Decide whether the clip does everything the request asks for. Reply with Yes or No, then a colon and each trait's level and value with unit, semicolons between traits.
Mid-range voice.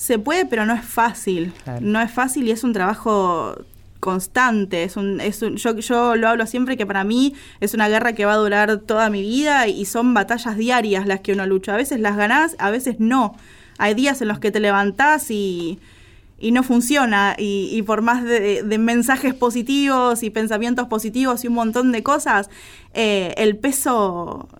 No: high, 220 Hz